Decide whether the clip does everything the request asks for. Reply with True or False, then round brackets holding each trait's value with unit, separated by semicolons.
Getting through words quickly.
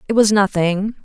False (175 wpm)